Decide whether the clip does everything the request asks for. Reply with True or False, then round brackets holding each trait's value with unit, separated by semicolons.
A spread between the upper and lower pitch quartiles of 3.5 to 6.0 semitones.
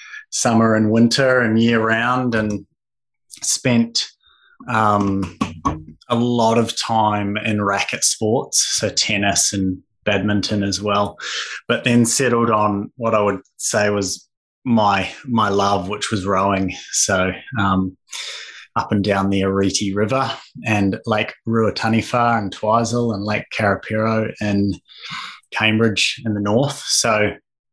False (2.7 semitones)